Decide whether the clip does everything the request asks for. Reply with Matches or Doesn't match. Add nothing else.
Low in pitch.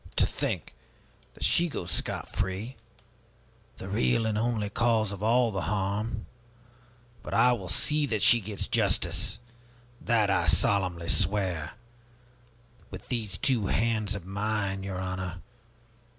Matches